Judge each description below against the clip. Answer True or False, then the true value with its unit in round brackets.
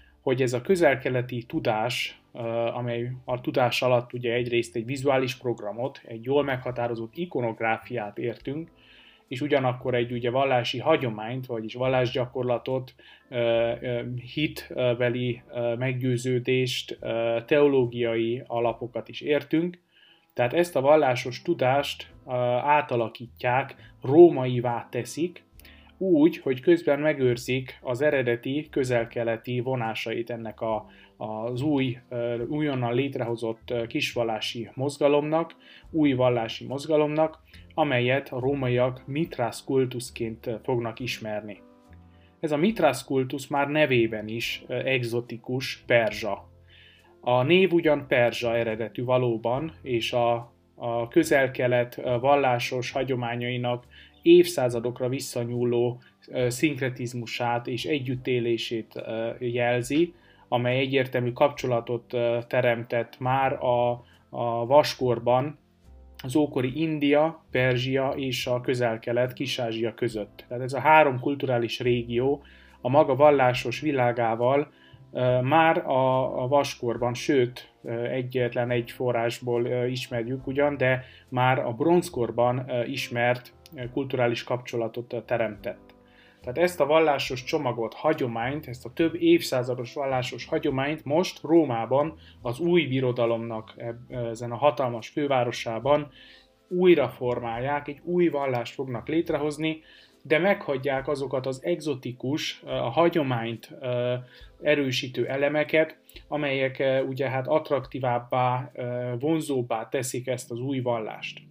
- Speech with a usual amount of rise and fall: True (3.0 semitones)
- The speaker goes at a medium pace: False (100 wpm)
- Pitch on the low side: True (125 Hz)